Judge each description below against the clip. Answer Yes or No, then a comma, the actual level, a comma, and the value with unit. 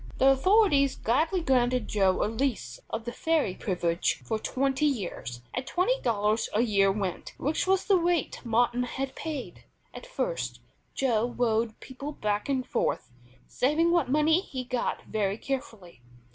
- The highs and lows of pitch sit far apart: Yes, wide, 5.7 semitones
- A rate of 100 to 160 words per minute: Yes, average, 155 wpm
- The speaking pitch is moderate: No, very high, 255 Hz